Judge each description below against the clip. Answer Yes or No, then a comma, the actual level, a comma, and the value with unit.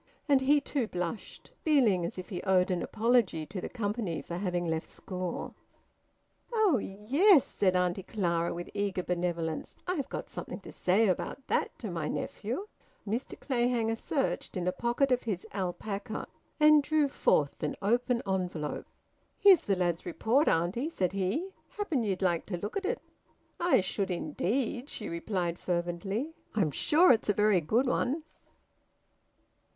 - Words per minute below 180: Yes, average, 155 wpm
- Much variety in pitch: Yes, wide, 6.2 semitones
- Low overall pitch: No, high, 205 Hz